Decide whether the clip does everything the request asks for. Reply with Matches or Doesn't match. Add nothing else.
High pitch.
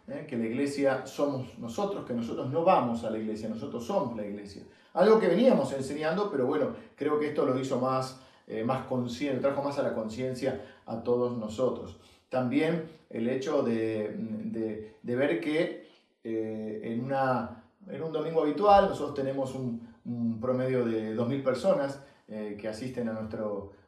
Doesn't match